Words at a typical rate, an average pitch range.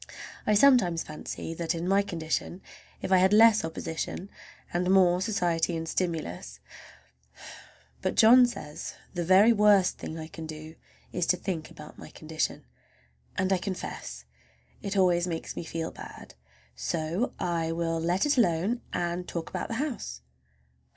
Yes: average, 150 wpm; average, 3.1 semitones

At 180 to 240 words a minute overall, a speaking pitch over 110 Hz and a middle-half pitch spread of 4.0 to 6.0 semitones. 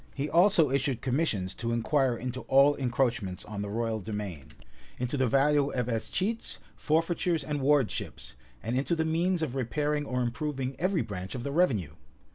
No: average, 165 wpm; low, 135 Hz; average, 4.4 semitones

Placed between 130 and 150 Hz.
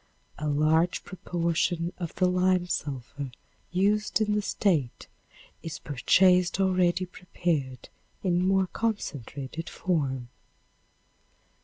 No: medium, 175 Hz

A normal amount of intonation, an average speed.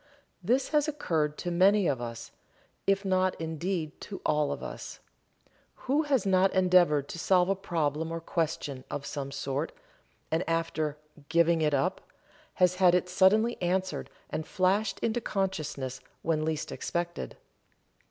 Yes: average, 3.8 semitones; average, 145 wpm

